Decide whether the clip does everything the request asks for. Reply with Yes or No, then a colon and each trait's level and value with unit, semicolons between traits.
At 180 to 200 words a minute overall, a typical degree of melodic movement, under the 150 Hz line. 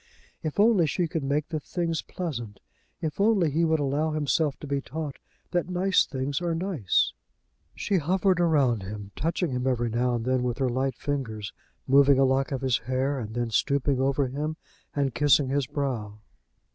Yes: average, 185 wpm; average, 3.9 semitones; medium, 140 Hz